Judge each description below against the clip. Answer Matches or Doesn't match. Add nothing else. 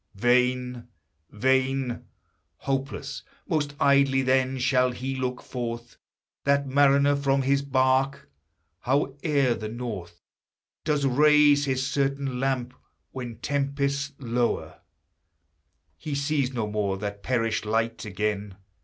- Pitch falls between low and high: Doesn't match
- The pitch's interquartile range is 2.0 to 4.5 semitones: Matches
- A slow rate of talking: Matches